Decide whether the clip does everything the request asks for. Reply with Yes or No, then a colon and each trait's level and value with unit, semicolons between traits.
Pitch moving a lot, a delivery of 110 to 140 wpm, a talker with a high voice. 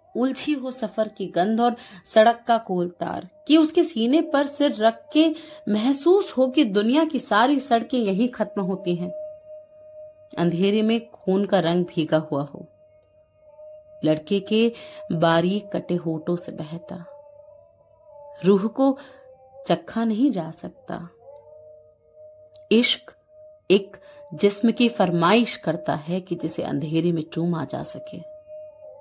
Yes: wide, 8.6 semitones; average, 130 wpm; high, 230 Hz